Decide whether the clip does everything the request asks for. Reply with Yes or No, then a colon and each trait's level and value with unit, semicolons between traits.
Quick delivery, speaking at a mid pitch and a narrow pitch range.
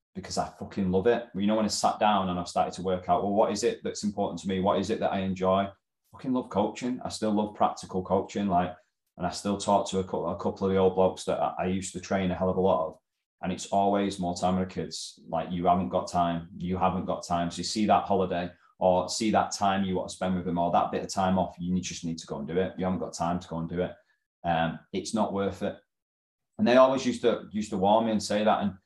No: fast, 290 wpm; very low, 95 Hz; narrow, 1.9 semitones